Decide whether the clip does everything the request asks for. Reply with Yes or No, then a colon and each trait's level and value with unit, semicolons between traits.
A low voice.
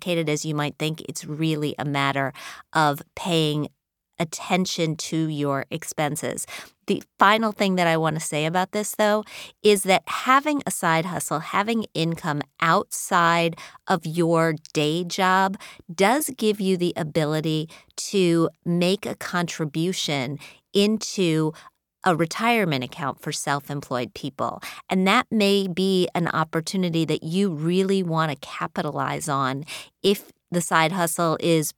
No: medium, 170 Hz